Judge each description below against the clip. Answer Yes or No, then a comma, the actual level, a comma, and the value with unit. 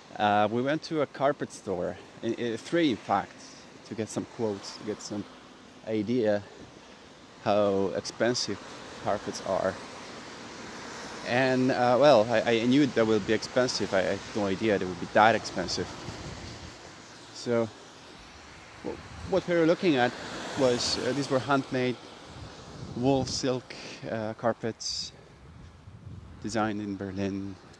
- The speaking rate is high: No, slow, 135 wpm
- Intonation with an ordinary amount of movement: Yes, average, 3.7 semitones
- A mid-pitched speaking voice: No, low, 115 Hz